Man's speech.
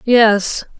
No: female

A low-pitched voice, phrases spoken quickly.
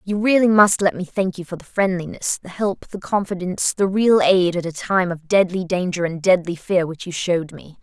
No: medium, 185 Hz; fast, 230 wpm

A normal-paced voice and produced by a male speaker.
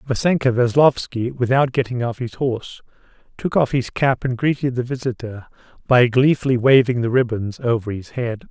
Yes: average, 160 wpm; male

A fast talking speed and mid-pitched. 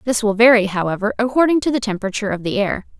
No: fast, 220 wpm; high, 220 Hz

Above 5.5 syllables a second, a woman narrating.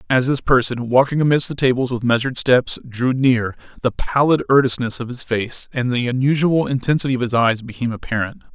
No: 5.7 syllables/s; male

